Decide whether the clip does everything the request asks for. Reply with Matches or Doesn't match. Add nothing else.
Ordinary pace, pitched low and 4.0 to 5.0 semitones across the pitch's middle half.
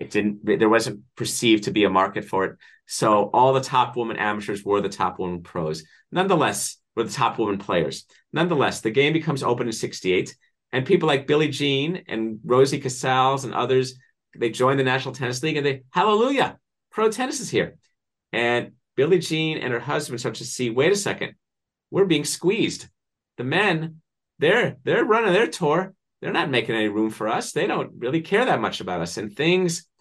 Doesn't match